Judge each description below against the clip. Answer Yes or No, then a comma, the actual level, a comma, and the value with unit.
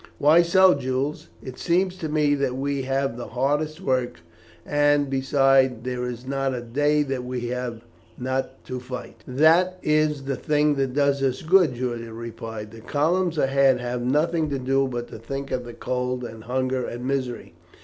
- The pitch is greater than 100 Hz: Yes, low, 135 Hz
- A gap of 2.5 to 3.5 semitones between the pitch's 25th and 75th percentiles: Yes, average, 2.8 semitones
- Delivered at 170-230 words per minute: Yes, average, 180 wpm